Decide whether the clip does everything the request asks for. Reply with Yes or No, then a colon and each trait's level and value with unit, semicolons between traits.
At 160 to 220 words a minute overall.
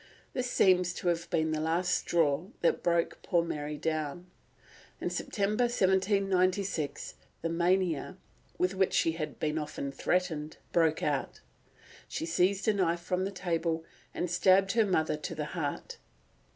No: average, 150 wpm